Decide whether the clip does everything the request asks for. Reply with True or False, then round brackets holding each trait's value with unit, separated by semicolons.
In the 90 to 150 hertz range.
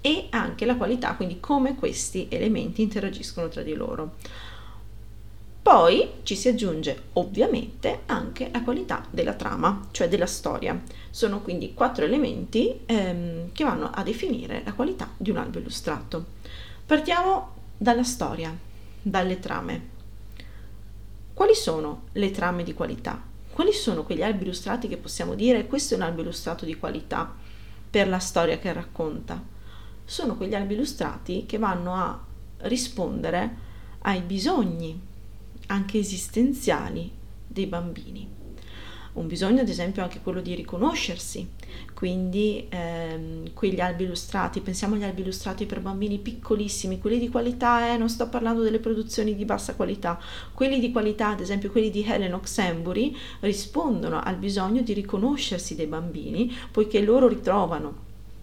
False (195 Hz)